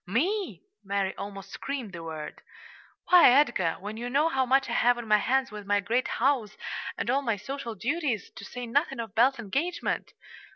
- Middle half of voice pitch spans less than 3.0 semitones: No, average, 5.0 semitones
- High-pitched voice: Yes, high, 240 Hz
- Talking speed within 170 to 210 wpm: Yes, average, 190 wpm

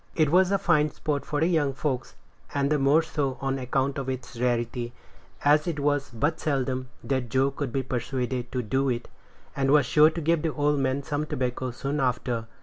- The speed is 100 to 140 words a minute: No, average, 200 wpm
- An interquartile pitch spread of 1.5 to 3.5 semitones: Yes, average, 2.7 semitones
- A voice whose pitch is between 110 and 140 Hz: Yes, low, 135 Hz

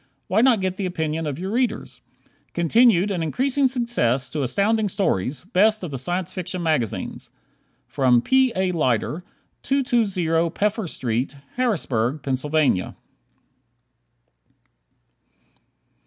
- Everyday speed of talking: No, slow, 110 wpm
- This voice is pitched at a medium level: Yes, medium, 180 Hz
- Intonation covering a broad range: Yes, wide, 6.6 semitones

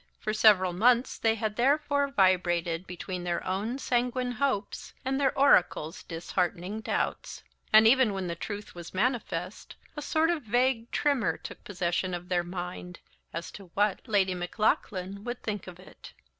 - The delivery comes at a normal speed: Yes, average, 155 wpm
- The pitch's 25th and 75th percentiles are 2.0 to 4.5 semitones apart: No, average, 5.3 semitones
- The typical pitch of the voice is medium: No, high, 205 Hz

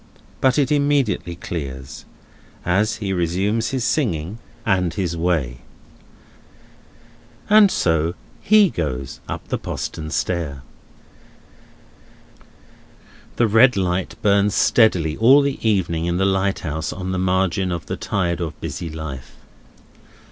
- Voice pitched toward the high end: No, very low, 90 Hz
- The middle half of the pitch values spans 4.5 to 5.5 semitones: Yes, average, 4.9 semitones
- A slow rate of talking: Yes, slow, 120 wpm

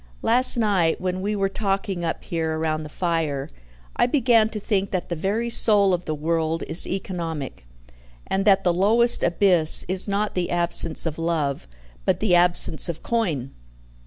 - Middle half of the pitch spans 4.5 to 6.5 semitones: No, average, 3.7 semitones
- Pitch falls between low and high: Yes, medium, 180 Hz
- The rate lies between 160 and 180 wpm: Yes, average, 170 wpm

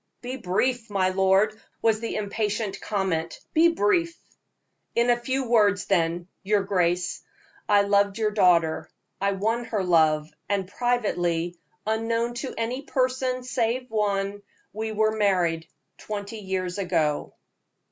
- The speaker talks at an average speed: No, slow, 130 wpm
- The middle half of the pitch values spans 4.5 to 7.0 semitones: No, average, 3.7 semitones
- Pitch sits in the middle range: No, high, 205 Hz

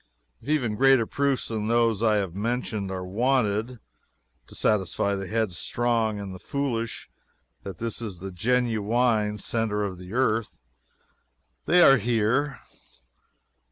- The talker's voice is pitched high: No, low, 110 Hz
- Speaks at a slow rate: Yes, slow, 130 wpm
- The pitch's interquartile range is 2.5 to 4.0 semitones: Yes, average, 3.2 semitones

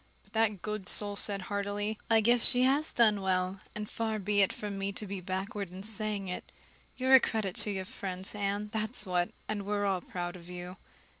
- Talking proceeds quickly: Yes, fast, 215 wpm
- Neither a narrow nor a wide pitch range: No, narrow, 2.1 semitones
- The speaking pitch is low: No, high, 205 Hz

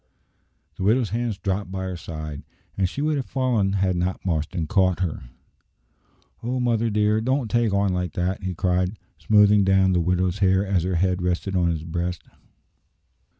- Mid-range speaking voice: No, very low, 95 Hz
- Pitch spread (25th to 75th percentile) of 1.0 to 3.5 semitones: Yes, average, 2.9 semitones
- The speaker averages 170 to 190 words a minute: Yes, average, 175 wpm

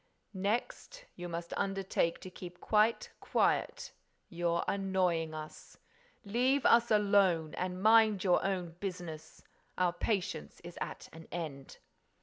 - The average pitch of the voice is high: No, medium, 180 Hz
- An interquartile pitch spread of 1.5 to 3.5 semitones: Yes, average, 3.1 semitones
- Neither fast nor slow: No, slow, 125 wpm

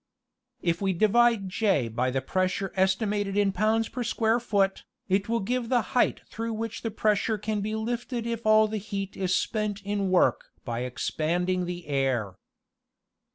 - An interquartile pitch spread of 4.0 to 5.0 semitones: No, average, 3.3 semitones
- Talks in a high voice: Yes, high, 205 Hz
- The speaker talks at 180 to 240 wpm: No, average, 165 wpm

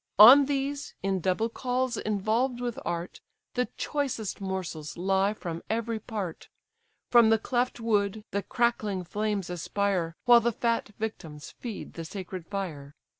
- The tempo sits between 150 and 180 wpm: No, average, 140 wpm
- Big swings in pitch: No, average, 4.2 semitones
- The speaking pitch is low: No, high, 210 Hz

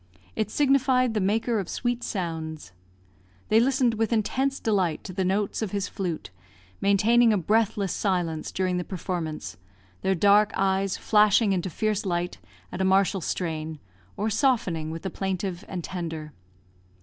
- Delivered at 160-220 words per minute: No, average, 150 wpm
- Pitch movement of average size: Yes, average, 3.8 semitones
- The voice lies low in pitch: No, high, 195 Hz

